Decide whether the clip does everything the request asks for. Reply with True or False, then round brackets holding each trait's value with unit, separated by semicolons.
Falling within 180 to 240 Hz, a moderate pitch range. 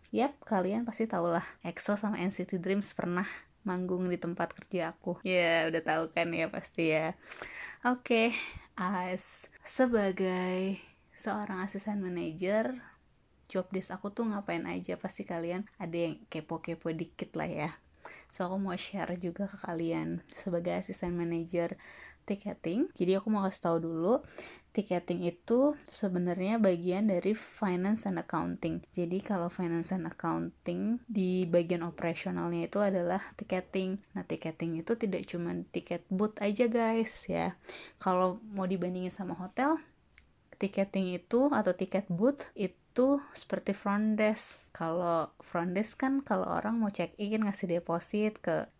True (185 Hz; 3.3 semitones)